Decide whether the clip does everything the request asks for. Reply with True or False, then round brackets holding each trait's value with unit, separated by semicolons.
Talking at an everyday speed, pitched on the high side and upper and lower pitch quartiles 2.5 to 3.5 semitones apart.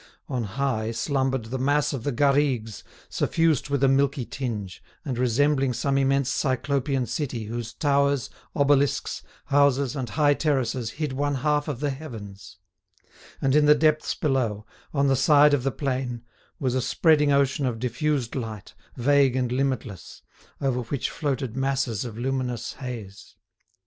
False (150 wpm; 135 Hz; 2.8 semitones)